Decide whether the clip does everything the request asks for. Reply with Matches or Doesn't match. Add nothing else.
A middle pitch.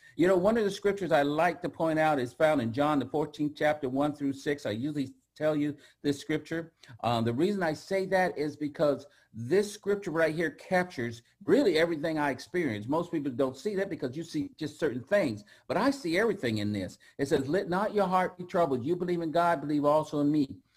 Matches